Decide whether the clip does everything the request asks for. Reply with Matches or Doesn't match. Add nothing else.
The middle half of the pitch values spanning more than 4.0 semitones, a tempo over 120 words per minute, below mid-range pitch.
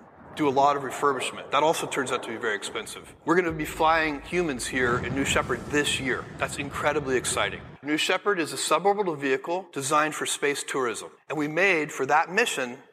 Doesn't match